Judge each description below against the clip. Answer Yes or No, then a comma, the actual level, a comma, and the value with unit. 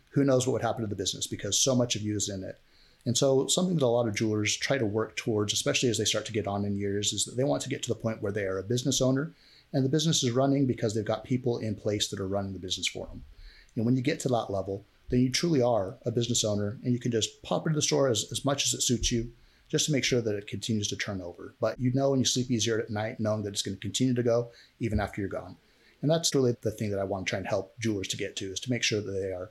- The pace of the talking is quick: Yes, fast, 310 wpm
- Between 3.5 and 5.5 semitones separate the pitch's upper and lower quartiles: Yes, average, 3.9 semitones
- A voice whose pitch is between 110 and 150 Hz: Yes, low, 115 Hz